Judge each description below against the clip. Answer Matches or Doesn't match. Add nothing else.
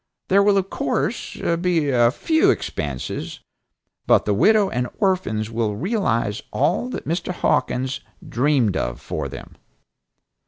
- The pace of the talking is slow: Matches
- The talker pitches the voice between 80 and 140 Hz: Matches